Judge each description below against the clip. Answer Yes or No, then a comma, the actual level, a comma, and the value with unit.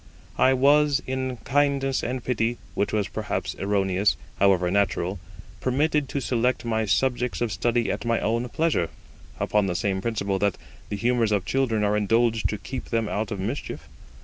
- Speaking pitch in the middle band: No, low, 115 Hz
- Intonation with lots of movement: No, average, 4.2 semitones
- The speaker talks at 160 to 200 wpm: Yes, average, 170 wpm